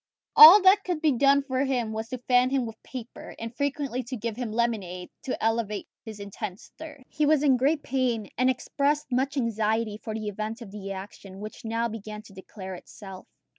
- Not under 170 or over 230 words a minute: Yes, average, 190 wpm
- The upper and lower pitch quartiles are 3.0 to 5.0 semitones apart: Yes, average, 4.1 semitones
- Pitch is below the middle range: No, high, 235 Hz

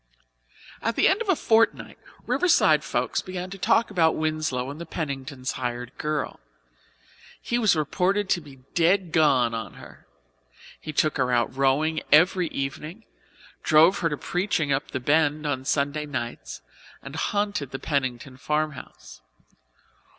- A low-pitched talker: No, medium, 150 Hz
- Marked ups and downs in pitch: No, average, 4.8 semitones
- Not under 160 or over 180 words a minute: No, average, 145 wpm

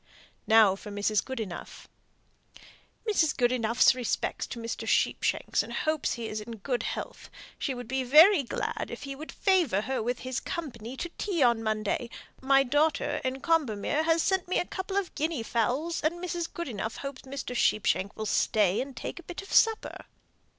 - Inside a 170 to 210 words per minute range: Yes, average, 175 wpm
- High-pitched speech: Yes, very high, 260 Hz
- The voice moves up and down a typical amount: No, wide, 6.2 semitones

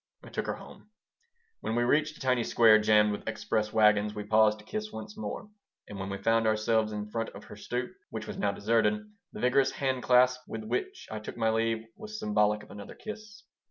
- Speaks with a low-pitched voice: Yes, low, 115 Hz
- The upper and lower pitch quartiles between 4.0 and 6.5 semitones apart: No, average, 3.6 semitones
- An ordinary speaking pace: No, fast, 215 wpm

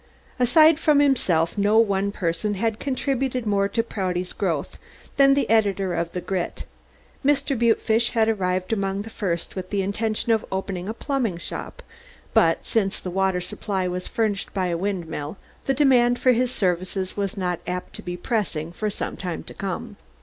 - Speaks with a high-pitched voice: Yes, high, 200 Hz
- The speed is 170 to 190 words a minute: Yes, average, 175 wpm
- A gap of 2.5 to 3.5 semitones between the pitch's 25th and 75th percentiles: No, average, 4.0 semitones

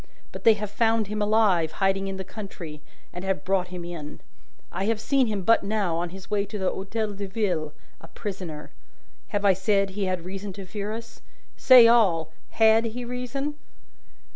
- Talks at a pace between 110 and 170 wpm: No, average, 190 wpm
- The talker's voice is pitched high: Yes, high, 200 Hz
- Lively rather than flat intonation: No, average, 3.0 semitones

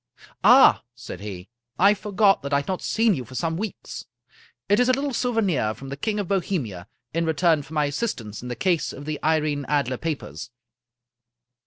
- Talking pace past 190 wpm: Yes, fast, 205 wpm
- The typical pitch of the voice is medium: Yes, medium, 160 Hz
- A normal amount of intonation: No, wide, 6.6 semitones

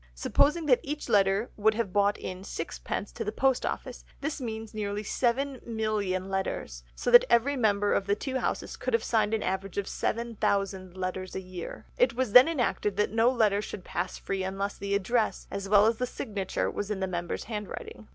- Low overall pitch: No, high, 210 Hz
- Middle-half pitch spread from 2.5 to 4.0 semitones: Yes, average, 3.4 semitones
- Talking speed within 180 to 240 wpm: Yes, average, 195 wpm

